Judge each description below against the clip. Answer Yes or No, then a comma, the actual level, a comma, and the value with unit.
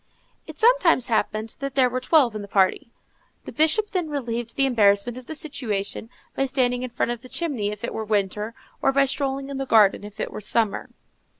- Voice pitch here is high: Yes, high, 245 Hz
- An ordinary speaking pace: No, fast, 210 wpm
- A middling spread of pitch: Yes, average, 4.4 semitones